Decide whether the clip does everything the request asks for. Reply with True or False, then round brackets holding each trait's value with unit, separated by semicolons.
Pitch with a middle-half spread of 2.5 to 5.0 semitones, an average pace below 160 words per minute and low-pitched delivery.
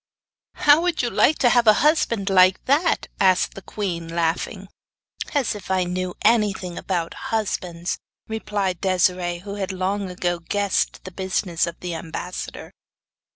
False (3.0 semitones; 150 wpm; 190 Hz)